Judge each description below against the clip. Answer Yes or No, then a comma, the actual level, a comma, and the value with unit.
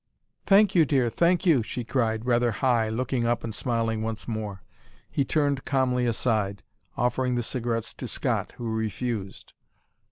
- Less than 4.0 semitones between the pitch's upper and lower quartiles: Yes, average, 2.7 semitones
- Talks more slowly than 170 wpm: Yes, average, 155 wpm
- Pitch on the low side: Yes, low, 120 Hz